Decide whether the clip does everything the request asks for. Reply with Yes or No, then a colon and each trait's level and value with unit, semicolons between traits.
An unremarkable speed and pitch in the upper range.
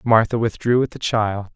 No: average, 195 wpm; low, 110 Hz